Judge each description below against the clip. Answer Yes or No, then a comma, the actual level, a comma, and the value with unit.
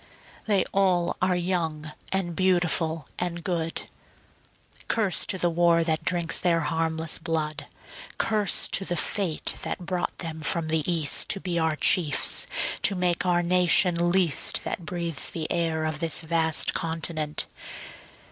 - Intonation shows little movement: Yes, narrow, 2.0 semitones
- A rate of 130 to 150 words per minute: Yes, average, 145 wpm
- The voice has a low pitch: No, medium, 170 Hz